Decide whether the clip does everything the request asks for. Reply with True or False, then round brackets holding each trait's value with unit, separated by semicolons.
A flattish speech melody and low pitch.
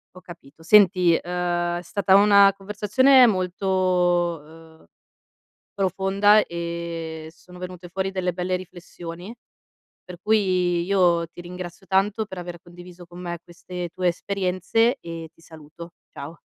False (2.0 semitones; 180 Hz)